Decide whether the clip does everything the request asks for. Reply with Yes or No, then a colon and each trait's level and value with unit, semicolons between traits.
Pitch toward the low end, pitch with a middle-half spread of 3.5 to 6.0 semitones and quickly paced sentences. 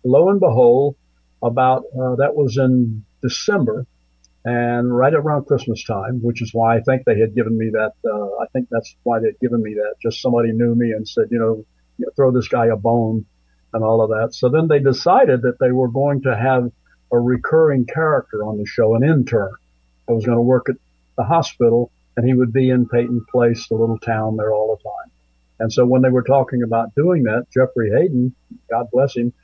No: low, 120 Hz; narrow, 2.4 semitones; fast, 215 wpm